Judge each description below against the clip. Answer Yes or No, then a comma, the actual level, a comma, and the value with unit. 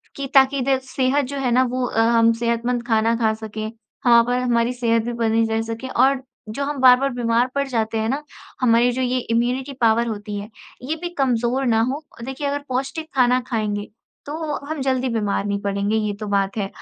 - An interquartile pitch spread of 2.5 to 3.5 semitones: Yes, average, 2.8 semitones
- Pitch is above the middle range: Yes, high, 240 Hz